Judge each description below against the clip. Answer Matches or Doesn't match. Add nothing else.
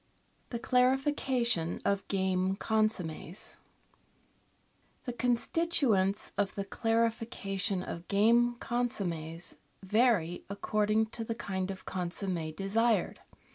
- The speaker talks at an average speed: Doesn't match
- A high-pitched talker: Matches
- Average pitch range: Matches